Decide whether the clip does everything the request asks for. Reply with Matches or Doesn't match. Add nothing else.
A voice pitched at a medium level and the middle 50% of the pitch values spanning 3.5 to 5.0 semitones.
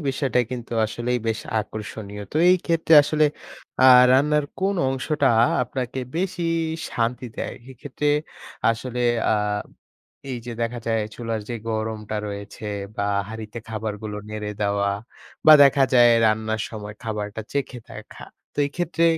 Doesn't match